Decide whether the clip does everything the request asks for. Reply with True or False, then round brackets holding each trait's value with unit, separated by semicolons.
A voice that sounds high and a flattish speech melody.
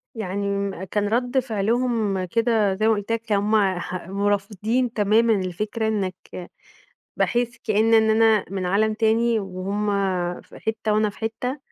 True (215 Hz; 2.2 semitones)